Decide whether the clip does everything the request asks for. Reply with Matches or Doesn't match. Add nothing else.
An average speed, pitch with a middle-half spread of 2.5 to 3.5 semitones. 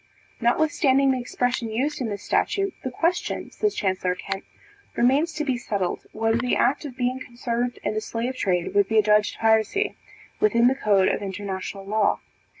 Doesn't match